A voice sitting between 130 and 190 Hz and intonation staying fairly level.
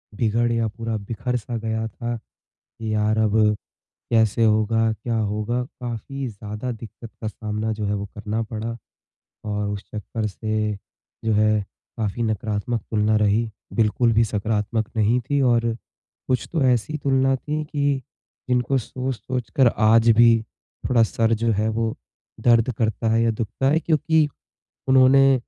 No: low, 115 Hz; narrow, 2.3 semitones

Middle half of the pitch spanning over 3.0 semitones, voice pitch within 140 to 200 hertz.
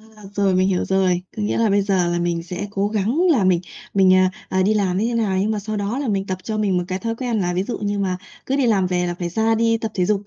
No: average, 2.7 semitones; high, 195 Hz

